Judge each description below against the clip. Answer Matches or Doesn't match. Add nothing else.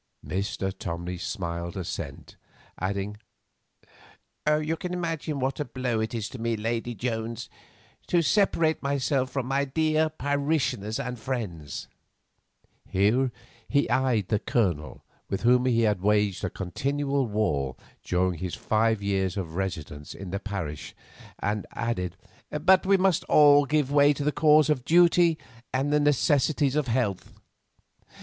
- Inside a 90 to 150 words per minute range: Matches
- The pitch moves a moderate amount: Doesn't match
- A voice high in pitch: Doesn't match